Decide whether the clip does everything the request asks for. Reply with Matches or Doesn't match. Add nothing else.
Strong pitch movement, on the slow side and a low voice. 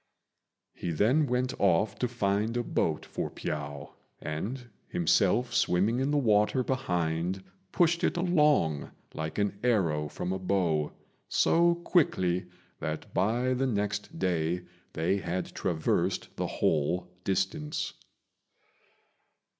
Matches